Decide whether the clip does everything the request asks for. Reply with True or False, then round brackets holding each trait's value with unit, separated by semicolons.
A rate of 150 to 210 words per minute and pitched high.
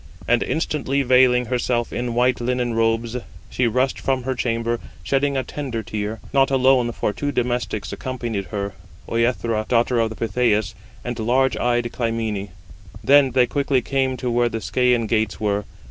False (160 wpm; 120 Hz)